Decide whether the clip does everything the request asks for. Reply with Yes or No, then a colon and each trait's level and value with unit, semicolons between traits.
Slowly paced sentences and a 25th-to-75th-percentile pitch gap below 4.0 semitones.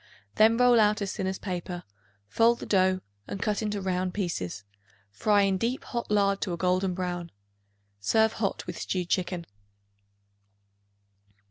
No: average, 150 wpm; average, 2.7 semitones